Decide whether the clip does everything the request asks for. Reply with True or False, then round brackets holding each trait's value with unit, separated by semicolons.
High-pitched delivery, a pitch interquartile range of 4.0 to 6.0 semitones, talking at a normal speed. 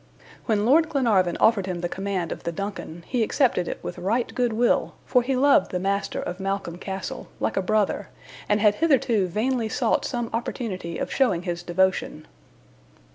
True (205 Hz; 4.6 semitones; 180 wpm)